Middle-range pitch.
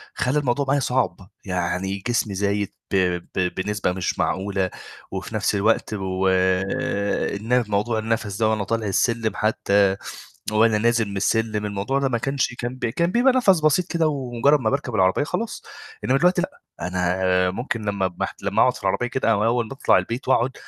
No: low, 110 Hz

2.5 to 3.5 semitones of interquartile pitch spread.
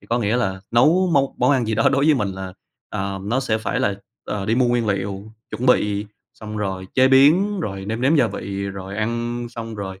No: average, 4.2 semitones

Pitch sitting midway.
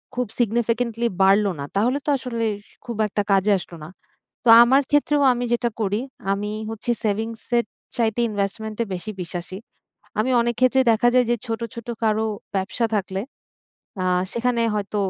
No: high, 225 Hz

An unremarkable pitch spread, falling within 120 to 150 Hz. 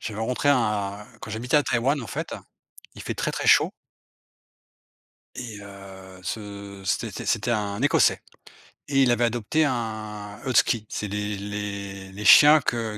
No: average, 3.1 semitones; low, 105 Hz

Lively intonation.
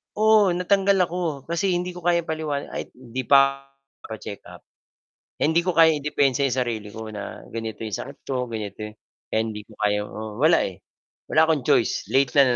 Yes: wide, 7.2 semitones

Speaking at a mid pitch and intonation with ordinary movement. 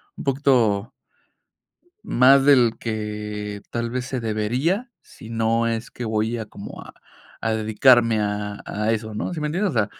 No: low, 115 Hz; average, 3.2 semitones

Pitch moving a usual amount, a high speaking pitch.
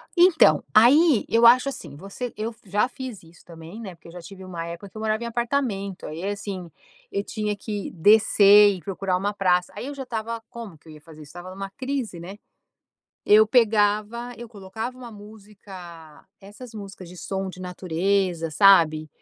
Yes: average, 3.8 semitones; high, 200 Hz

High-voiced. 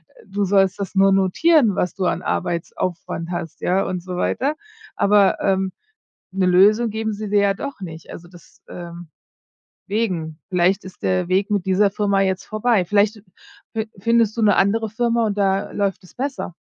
Yes: high, 195 Hz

